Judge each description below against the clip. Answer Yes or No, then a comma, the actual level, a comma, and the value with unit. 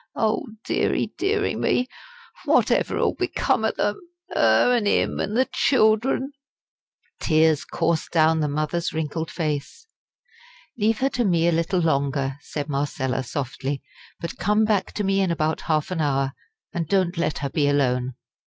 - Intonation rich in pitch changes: Yes, wide, 6.1 semitones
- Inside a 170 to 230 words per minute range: No, average, 160 wpm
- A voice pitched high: No, medium, 165 Hz